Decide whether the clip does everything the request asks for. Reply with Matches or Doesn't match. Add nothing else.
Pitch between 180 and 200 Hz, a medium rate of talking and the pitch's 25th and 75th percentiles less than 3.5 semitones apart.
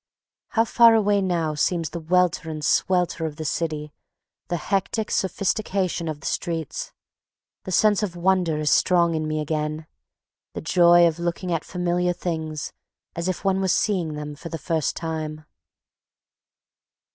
Doesn't match